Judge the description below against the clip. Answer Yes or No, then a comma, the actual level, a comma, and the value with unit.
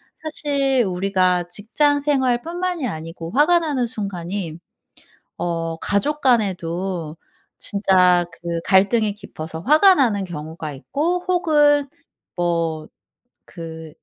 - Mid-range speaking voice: No, high, 200 Hz